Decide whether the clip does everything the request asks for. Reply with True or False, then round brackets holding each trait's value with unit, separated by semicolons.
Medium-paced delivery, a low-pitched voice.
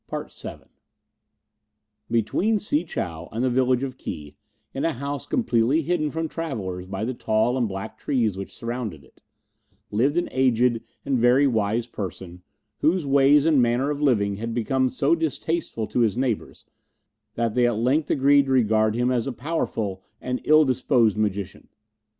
True (165 wpm; 125 Hz)